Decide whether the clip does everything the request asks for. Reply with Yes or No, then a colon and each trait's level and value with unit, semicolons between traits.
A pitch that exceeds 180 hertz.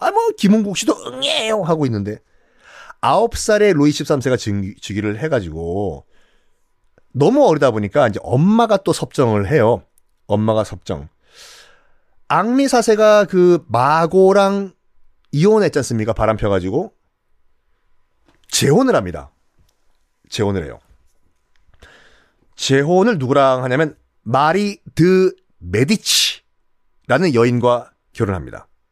No: low, 130 Hz